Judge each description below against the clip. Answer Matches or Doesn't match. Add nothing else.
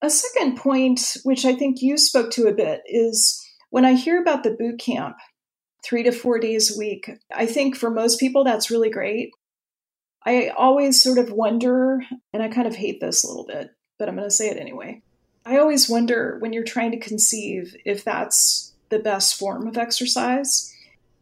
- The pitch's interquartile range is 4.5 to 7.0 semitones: Doesn't match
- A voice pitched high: Matches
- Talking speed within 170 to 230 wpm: Matches